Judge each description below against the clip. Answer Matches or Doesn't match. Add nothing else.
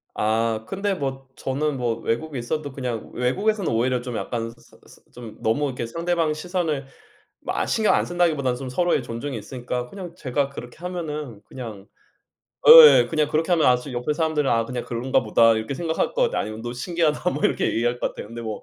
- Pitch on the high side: Doesn't match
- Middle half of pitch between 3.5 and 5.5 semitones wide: Matches